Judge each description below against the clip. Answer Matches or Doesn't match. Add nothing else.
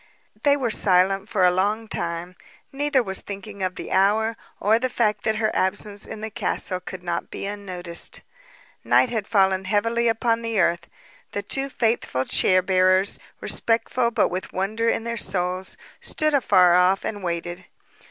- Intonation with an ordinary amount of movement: Matches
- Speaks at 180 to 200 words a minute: Doesn't match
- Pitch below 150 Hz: Doesn't match